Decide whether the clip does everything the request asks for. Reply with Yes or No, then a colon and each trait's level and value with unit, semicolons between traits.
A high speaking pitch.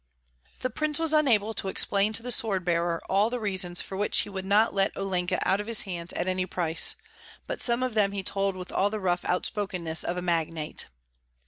Yes: high, 195 Hz